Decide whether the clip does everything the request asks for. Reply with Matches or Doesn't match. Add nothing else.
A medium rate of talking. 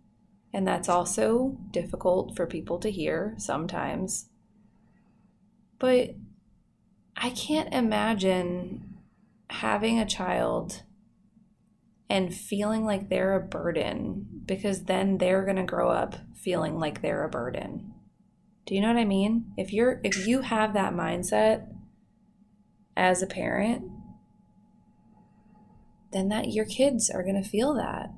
Doesn't match